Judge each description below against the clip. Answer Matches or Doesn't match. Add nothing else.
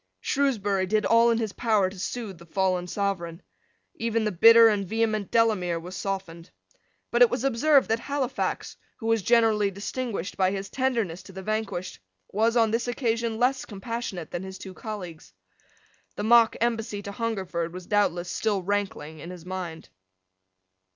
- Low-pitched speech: Doesn't match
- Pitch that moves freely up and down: Doesn't match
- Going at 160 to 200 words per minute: Matches